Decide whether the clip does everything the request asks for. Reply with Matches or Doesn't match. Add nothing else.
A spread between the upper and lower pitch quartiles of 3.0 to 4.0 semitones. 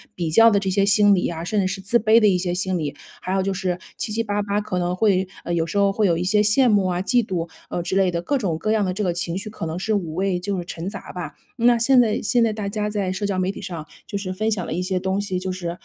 Doesn't match